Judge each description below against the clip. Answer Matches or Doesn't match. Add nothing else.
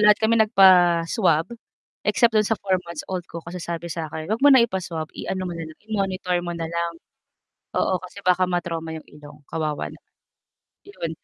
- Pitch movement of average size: Matches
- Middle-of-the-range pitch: Matches